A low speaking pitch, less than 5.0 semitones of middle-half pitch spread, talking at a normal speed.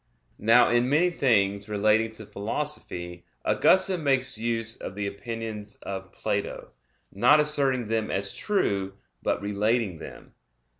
No: low, 110 Hz; average, 4.3 semitones; slow, 130 wpm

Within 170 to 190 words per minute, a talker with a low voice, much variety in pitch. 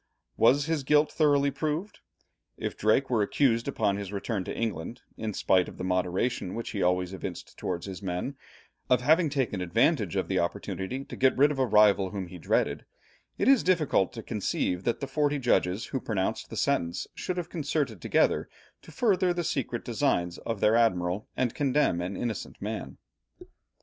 Yes: average, 180 wpm; low, 115 Hz; wide, 7.0 semitones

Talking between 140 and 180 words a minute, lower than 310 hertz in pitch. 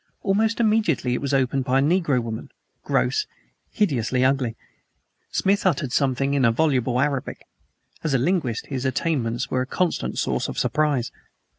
Yes: average, 150 wpm; low, 135 Hz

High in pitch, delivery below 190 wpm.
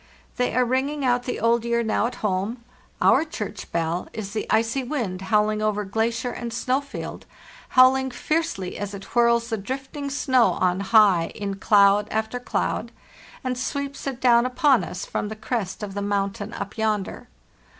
Yes: high, 230 Hz; average, 170 wpm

